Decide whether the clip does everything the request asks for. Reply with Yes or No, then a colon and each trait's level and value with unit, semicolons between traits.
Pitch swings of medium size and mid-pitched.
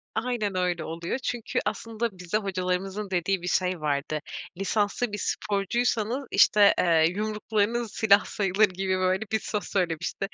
No: average, 3.0 semitones; high, 195 Hz